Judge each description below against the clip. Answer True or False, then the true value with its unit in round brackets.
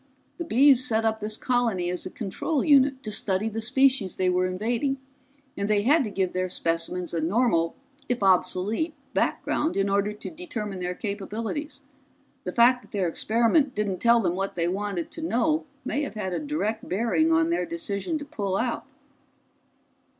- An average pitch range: False (6.0 semitones)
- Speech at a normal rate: True (180 wpm)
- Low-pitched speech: False (220 Hz)